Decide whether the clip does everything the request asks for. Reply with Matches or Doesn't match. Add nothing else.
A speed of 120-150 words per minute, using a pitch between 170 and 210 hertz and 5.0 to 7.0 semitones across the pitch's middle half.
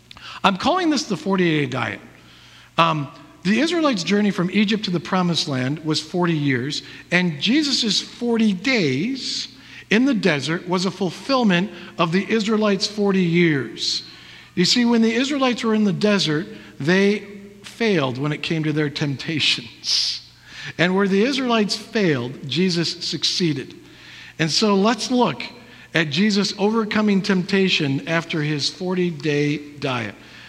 Matches